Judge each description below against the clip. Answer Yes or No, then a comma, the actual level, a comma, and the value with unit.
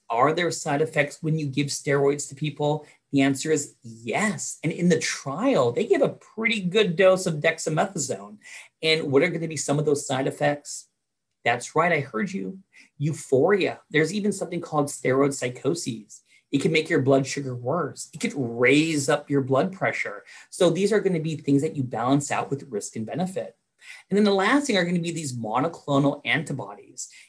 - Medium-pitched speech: Yes, medium, 150 Hz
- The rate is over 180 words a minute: Yes, average, 200 wpm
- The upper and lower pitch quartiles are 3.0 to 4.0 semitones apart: Yes, average, 3.5 semitones